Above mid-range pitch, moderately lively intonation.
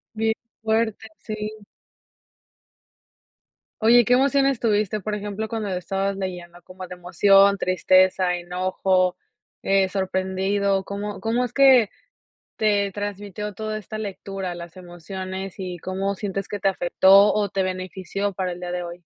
No: high, 195 Hz; narrow, 2.2 semitones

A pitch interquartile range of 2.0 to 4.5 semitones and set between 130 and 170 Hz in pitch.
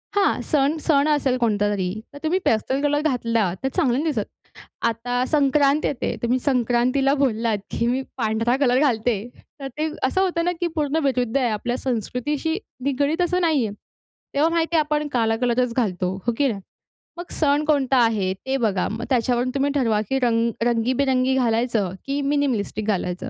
No: average, 3.9 semitones; very high, 255 Hz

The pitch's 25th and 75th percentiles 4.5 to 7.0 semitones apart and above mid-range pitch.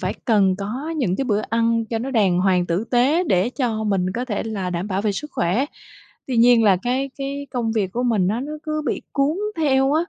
Yes: average, 5.2 semitones; high, 230 Hz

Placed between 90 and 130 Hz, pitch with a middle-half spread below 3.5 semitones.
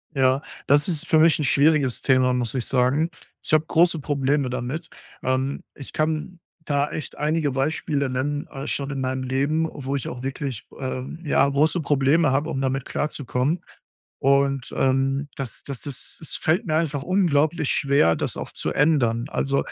No: medium, 140 Hz; average, 2.7 semitones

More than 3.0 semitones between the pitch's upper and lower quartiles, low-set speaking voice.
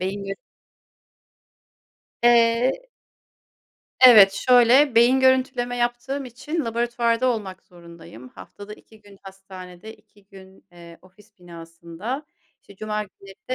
No: average, 4.3 semitones; high, 215 Hz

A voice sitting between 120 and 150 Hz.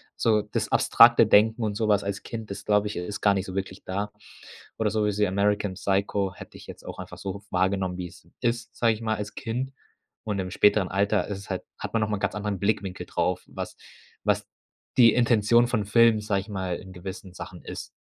No: low, 105 Hz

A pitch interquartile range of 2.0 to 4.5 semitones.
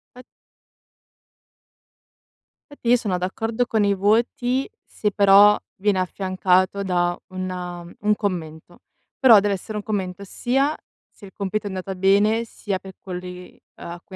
Yes: narrow, 2.5 semitones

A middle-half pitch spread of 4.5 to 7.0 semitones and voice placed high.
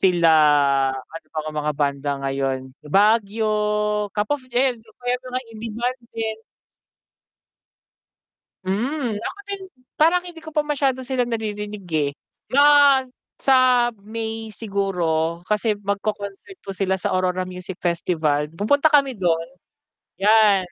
Yes: wide, 5.4 semitones; high, 210 Hz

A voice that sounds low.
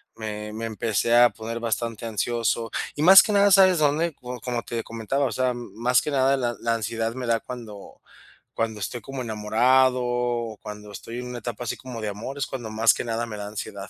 Yes: low, 115 Hz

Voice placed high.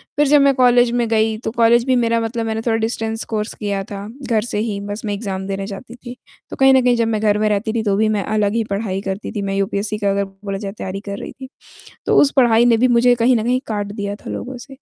Yes: high, 220 Hz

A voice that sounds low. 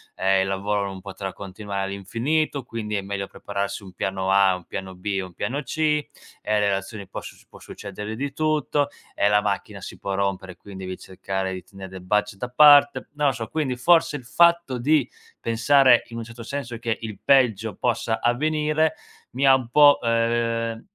Yes: low, 115 Hz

